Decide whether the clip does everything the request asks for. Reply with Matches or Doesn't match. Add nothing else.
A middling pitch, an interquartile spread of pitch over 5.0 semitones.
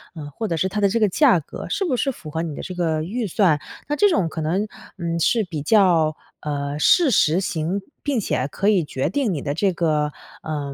Matches